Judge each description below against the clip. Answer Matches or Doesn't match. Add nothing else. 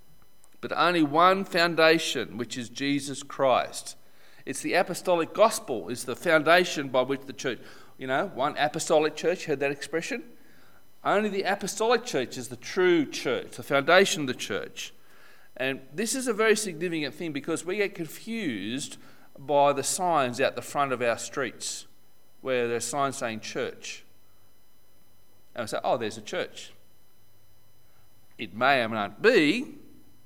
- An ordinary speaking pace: Matches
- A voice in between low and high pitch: Matches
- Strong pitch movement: Matches